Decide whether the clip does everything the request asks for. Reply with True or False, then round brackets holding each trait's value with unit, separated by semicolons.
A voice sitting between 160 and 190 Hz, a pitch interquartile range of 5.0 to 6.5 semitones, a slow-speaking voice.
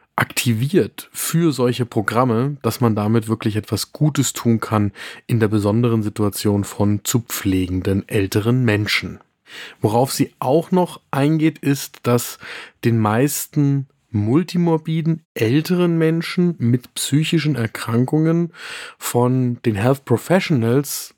False (125 Hz; 5.5 semitones; 115 wpm)